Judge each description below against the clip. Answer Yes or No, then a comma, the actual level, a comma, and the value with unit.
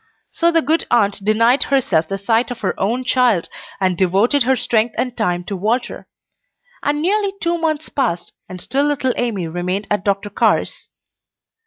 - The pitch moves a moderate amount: No, wide, 5.8 semitones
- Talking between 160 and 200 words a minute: Yes, average, 170 wpm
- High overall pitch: Yes, high, 230 Hz